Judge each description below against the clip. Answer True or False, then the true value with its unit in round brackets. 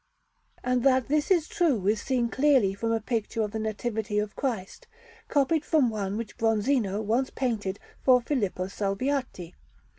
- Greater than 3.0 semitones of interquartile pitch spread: True (4.3 semitones)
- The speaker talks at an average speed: True (155 wpm)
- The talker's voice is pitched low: False (230 Hz)